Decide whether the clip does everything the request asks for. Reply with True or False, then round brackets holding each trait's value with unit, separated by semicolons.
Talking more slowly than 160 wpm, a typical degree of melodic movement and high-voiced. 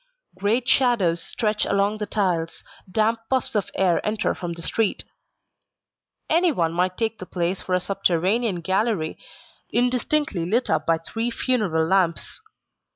True (140 wpm; 4.7 semitones; 195 Hz)